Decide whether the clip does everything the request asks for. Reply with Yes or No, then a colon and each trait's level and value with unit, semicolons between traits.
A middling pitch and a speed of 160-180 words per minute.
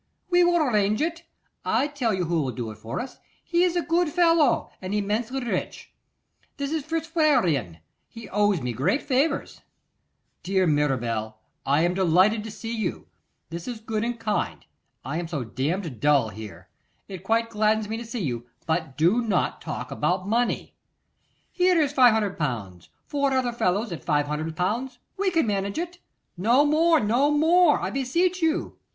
No: high, 215 Hz; average, 165 wpm